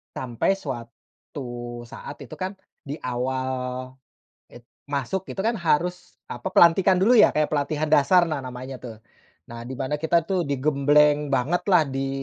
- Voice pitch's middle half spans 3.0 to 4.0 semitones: No, average, 4.8 semitones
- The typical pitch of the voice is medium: Yes, medium, 145 Hz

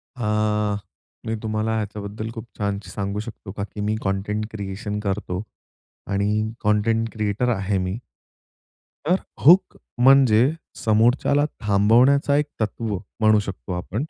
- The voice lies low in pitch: Yes, low, 105 Hz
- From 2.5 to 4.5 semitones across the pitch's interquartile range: No, narrow, 1.9 semitones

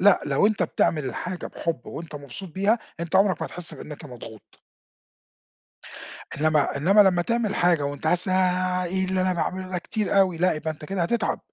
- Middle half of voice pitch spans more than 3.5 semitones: No, average, 3.2 semitones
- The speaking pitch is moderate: Yes, medium, 180 Hz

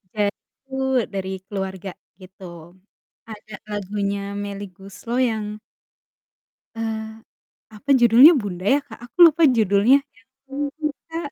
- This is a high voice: Yes, high, 215 Hz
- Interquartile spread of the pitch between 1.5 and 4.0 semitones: No, average, 4.5 semitones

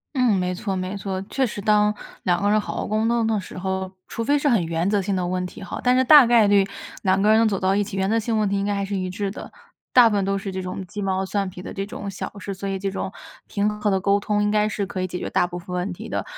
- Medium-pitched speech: No, high, 200 Hz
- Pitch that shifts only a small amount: Yes, narrow, 2.0 semitones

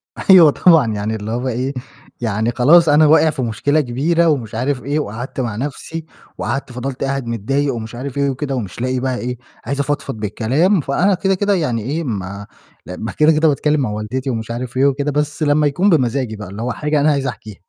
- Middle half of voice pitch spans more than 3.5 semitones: Yes, average, 4.3 semitones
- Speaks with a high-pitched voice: No, low, 135 Hz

